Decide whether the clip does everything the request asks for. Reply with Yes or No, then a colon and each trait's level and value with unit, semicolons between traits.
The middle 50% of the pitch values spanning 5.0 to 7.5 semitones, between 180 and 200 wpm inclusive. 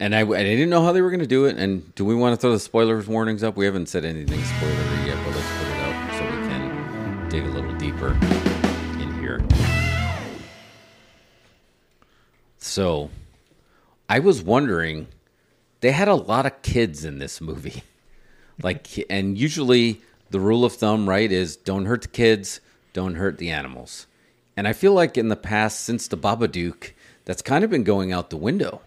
Yes: wide, 5.6 semitones; average, 185 wpm